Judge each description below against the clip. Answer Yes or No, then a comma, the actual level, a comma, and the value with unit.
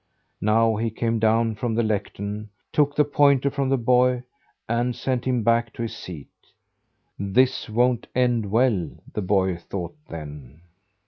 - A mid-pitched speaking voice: No, low, 115 Hz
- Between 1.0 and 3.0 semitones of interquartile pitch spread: No, average, 3.6 semitones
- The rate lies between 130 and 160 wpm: Yes, average, 150 wpm